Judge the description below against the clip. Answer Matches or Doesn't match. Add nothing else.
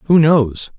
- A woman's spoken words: Doesn't match